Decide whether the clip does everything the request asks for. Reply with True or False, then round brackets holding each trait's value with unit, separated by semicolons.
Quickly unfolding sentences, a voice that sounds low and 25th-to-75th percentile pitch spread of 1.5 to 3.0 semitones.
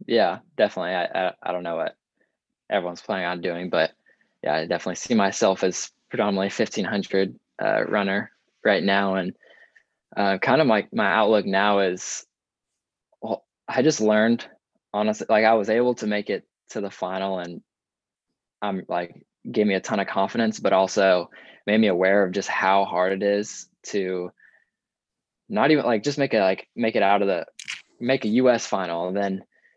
False (180 wpm; 100 Hz; 2.4 semitones)